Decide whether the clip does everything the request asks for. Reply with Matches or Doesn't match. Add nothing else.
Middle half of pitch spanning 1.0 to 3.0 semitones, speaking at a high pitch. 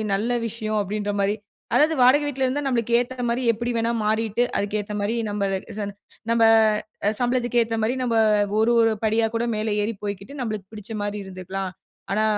Matches